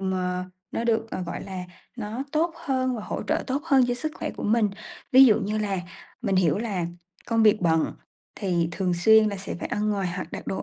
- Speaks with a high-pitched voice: Yes, high, 210 Hz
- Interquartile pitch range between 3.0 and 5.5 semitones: Yes, average, 4.1 semitones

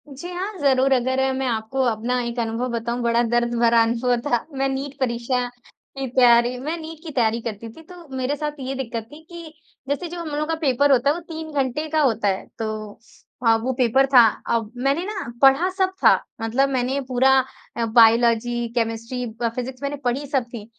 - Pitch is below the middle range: No, very high, 255 Hz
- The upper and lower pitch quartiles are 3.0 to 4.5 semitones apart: Yes, average, 3.4 semitones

